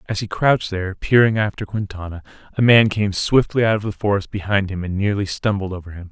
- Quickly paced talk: Yes, fast, 215 wpm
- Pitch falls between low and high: No, low, 100 Hz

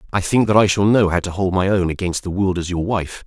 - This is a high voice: No, very low, 95 Hz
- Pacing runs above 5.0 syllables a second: Yes, 6.0 syllables/s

